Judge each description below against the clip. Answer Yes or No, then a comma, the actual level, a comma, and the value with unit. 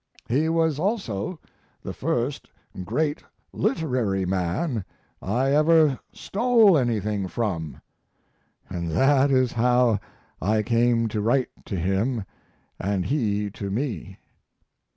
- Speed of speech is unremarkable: No, slow, 110 wpm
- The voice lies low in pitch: Yes, low, 120 Hz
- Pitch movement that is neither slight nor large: No, wide, 6.3 semitones